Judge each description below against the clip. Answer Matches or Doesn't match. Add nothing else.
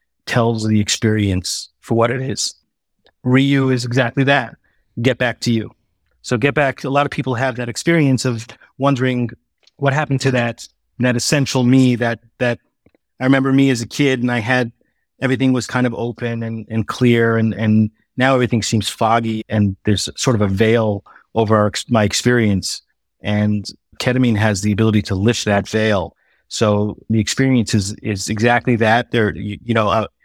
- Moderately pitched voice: Doesn't match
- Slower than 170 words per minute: Doesn't match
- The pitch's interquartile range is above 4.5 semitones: Doesn't match